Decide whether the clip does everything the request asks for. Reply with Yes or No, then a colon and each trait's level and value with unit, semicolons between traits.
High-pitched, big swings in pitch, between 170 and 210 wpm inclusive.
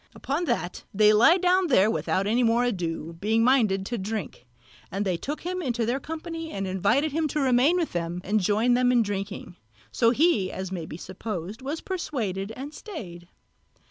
Yes: high, 225 Hz; wide, 6.8 semitones; average, 185 wpm